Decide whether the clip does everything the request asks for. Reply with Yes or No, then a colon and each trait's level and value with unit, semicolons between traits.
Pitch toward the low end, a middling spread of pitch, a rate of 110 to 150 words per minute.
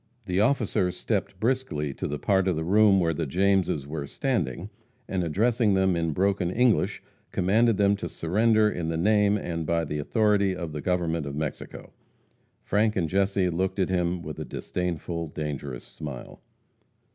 No: very low, 90 Hz; average, 4.0 semitones; average, 170 wpm